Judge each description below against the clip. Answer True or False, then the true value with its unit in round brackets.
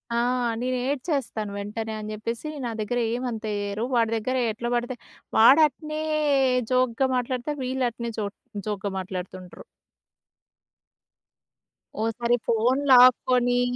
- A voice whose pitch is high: True (240 Hz)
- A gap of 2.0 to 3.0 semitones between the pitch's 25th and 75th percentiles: True (2.7 semitones)